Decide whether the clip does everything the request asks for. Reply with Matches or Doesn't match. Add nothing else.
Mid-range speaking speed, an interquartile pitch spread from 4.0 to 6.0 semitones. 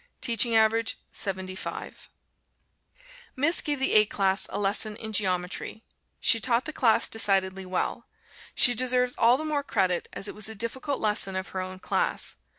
Matches